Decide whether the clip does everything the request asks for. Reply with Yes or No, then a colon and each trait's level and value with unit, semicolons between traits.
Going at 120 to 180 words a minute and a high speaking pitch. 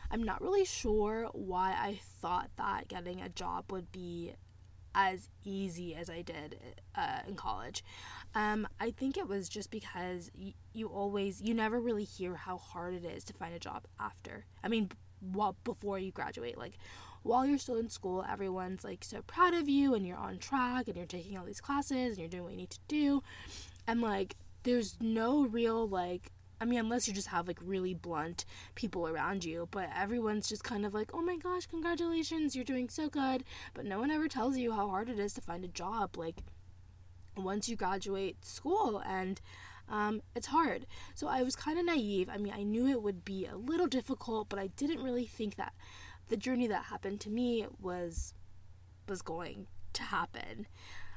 No: average, 195 wpm; high, 200 Hz